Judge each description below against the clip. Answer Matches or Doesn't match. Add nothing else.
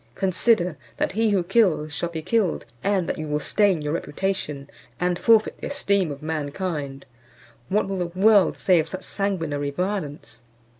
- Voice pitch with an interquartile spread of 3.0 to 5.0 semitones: Matches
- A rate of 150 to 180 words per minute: Matches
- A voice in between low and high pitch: Matches